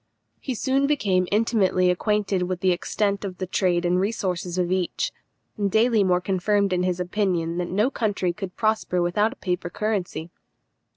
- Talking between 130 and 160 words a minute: No, average, 170 wpm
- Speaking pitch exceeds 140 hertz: Yes, medium, 185 Hz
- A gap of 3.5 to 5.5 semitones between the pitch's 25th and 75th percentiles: No, average, 2.9 semitones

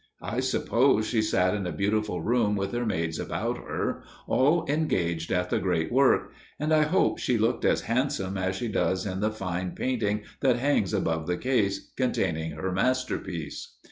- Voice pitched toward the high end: No, low, 105 Hz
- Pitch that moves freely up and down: Yes, wide, 5.7 semitones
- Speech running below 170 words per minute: No, average, 175 wpm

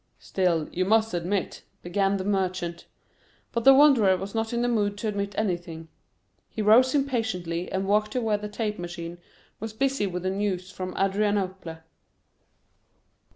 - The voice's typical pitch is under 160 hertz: No, high, 200 Hz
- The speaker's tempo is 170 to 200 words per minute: No, average, 155 wpm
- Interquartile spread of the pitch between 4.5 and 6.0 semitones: No, average, 3.2 semitones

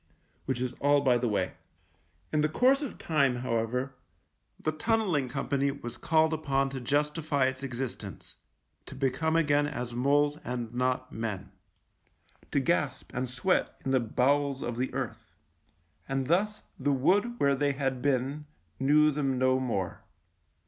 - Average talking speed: Yes, average, 160 wpm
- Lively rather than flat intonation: No, average, 2.9 semitones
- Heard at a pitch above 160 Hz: No, low, 135 Hz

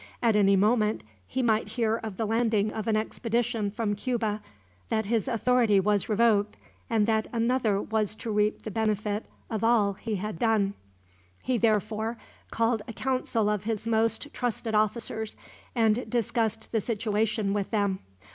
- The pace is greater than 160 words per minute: No, average, 155 wpm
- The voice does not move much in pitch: Yes, narrow, 1.6 semitones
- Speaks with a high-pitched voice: Yes, high, 220 Hz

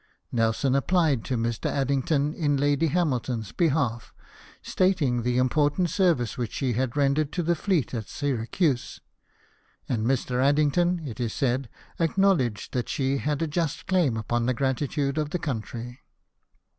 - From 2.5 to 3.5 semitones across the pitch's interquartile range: No, average, 4.2 semitones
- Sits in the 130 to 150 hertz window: Yes, medium, 140 Hz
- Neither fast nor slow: Yes, average, 150 wpm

